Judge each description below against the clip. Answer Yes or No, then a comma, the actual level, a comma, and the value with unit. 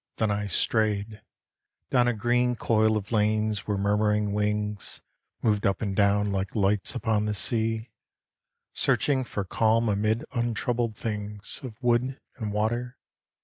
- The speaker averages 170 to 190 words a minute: No, average, 140 wpm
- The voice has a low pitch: Yes, low, 110 Hz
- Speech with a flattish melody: Yes, narrow, 2.1 semitones